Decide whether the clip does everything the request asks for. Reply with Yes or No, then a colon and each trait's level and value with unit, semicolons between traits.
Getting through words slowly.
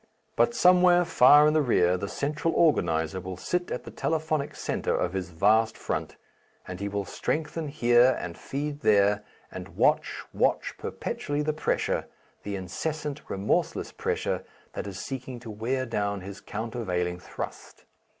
No: average, 150 wpm